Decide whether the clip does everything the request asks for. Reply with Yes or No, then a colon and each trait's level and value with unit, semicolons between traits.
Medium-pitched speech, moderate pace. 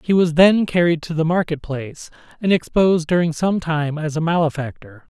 Yes: medium, 165 Hz; average, 185 wpm